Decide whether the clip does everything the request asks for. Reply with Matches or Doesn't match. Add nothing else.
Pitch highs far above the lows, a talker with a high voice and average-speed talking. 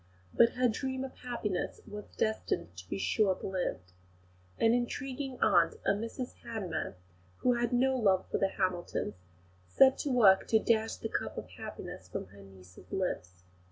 Matches